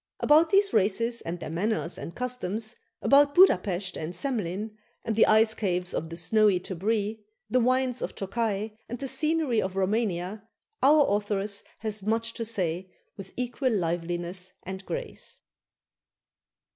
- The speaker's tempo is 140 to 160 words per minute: Yes, average, 150 wpm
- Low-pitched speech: No, high, 215 Hz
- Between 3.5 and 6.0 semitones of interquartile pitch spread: Yes, average, 4.6 semitones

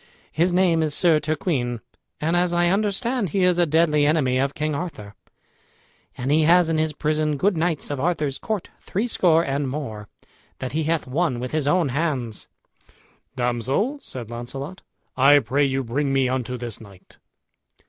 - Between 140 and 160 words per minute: No, average, 170 wpm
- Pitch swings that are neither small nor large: Yes, average, 4.7 semitones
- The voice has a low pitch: No, medium, 150 Hz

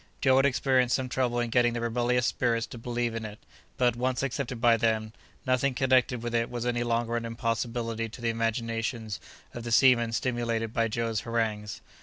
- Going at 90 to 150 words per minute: No, average, 190 wpm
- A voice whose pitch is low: Yes, low, 120 Hz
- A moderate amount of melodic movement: No, narrow, 1.3 semitones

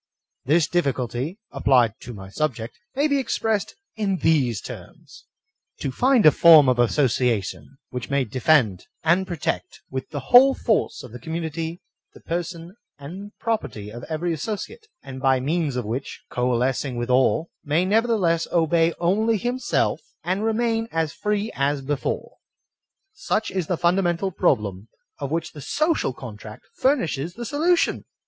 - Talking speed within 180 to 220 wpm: No, average, 155 wpm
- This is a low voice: No, medium, 160 Hz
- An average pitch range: No, wide, 7.4 semitones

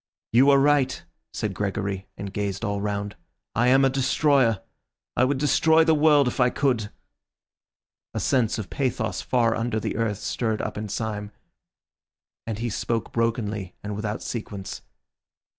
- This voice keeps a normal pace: Yes, average, 160 wpm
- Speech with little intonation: No, average, 4.3 semitones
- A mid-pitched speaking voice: No, low, 115 Hz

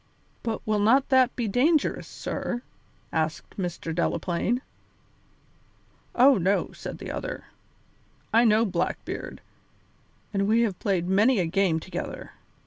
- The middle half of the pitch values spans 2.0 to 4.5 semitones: No, average, 5.1 semitones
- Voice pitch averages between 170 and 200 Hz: No, high, 210 Hz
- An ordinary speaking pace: No, slow, 125 wpm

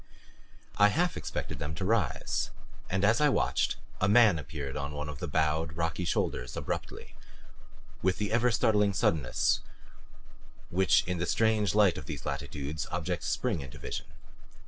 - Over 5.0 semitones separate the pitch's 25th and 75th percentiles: Yes, wide, 5.5 semitones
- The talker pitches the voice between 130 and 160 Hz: No, very low, 90 Hz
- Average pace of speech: Yes, average, 155 wpm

